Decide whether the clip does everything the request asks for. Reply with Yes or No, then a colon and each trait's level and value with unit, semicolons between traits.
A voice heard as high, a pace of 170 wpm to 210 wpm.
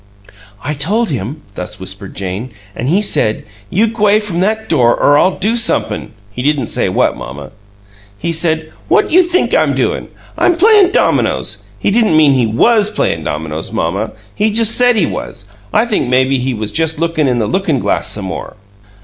No: medium, 155 Hz; average, 185 wpm